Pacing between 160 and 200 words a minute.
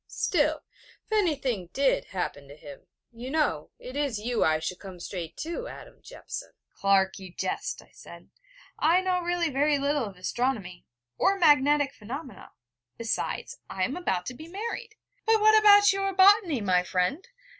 Yes: average, 165 wpm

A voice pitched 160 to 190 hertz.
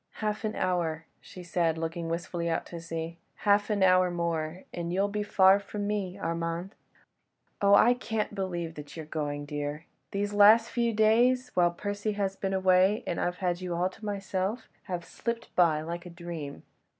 Yes: medium, 185 Hz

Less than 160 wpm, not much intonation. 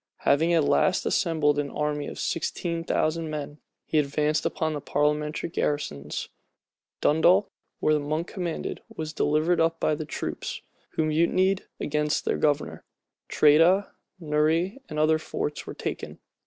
Yes: average, 140 wpm; narrow, 1.9 semitones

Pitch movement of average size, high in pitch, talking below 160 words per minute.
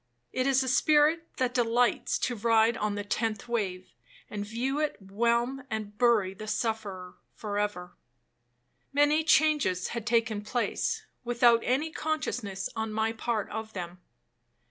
Yes: average, 3.6 semitones; high, 230 Hz; average, 145 wpm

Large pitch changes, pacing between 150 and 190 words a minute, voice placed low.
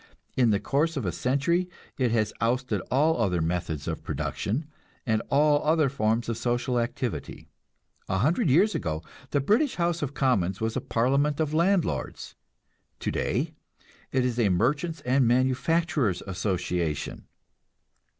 No: wide, 5.9 semitones; average, 140 wpm; low, 130 Hz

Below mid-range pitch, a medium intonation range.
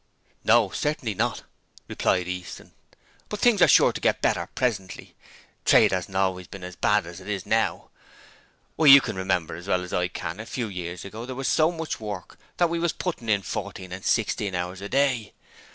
No: low, 100 Hz; wide, 5.7 semitones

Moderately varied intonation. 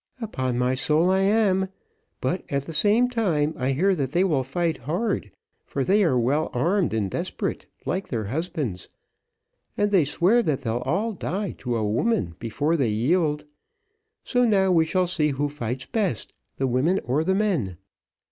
No: wide, 6.7 semitones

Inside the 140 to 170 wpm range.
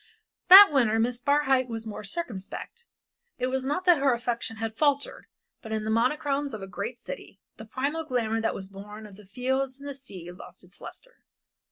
No: average, 200 wpm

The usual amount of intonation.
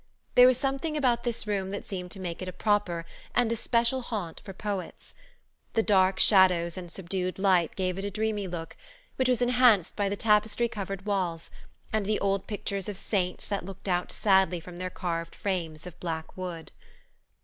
Yes: average, 3.1 semitones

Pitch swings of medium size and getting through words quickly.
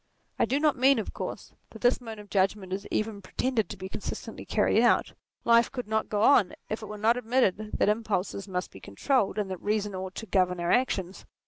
Yes: average, 3.5 semitones; fast, 225 wpm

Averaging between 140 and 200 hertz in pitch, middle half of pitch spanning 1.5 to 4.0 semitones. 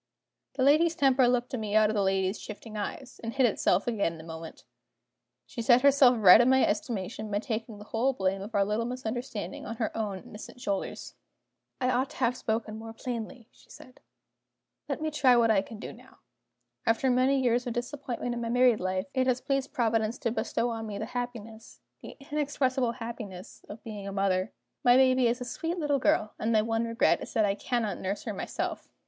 No: high, 230 Hz; average, 3.2 semitones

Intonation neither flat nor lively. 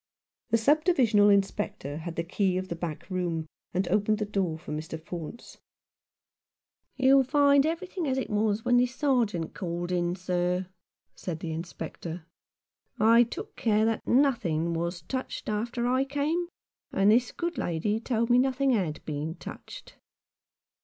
No: wide, 6.5 semitones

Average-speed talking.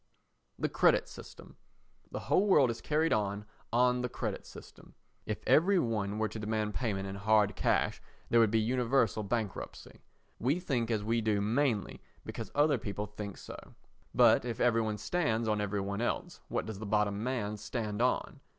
Yes: average, 180 wpm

